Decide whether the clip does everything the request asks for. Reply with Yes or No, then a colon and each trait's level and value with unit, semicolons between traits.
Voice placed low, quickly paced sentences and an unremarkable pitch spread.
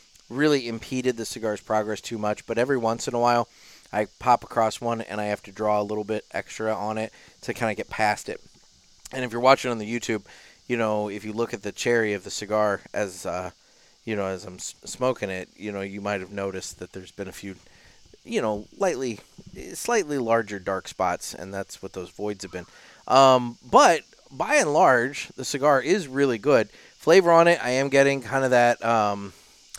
Yes: low, 110 Hz; fast, 210 wpm; average, 3.2 semitones